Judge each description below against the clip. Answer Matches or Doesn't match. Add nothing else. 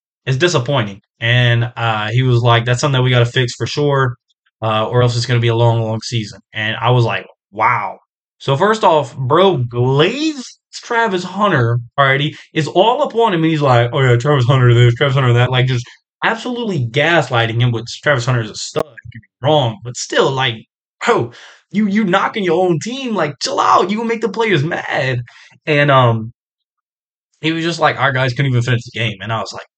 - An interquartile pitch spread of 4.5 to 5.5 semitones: Matches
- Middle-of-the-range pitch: Doesn't match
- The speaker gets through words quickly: Matches